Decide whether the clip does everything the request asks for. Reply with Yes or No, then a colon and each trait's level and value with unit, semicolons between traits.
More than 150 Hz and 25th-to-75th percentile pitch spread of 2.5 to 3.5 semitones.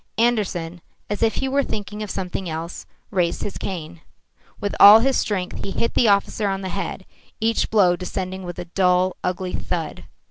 Yes: high, 190 Hz; average, 2.8 semitones